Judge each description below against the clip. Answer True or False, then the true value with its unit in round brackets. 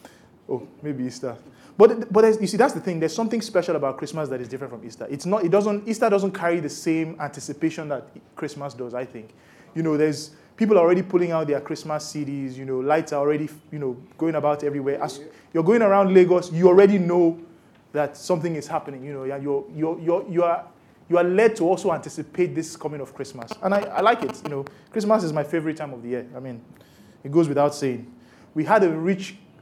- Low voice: False (155 Hz)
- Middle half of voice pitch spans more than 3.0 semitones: True (4.0 semitones)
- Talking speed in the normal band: False (225 wpm)